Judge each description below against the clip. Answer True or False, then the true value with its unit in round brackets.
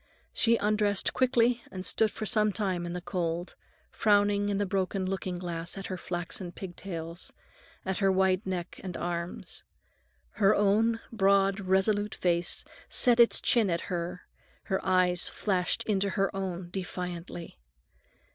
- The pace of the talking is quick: False (145 wpm)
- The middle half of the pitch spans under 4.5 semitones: True (2.4 semitones)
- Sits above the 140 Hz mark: True (190 Hz)